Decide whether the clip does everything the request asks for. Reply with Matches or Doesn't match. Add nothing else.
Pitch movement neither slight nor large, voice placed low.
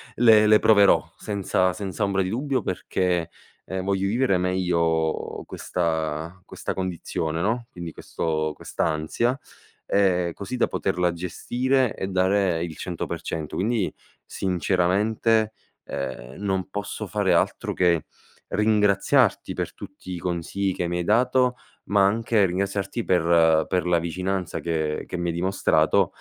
Matches